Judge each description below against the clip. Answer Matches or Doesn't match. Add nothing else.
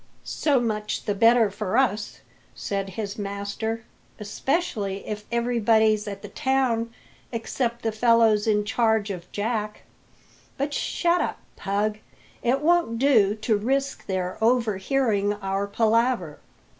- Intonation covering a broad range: Doesn't match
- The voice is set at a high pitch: Matches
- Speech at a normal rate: Doesn't match